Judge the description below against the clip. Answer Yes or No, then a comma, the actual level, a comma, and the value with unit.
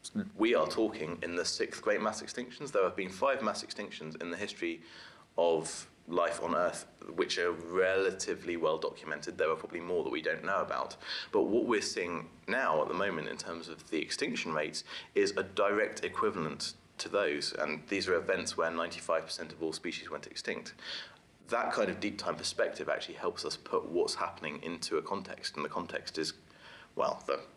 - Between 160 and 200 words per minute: Yes, average, 190 wpm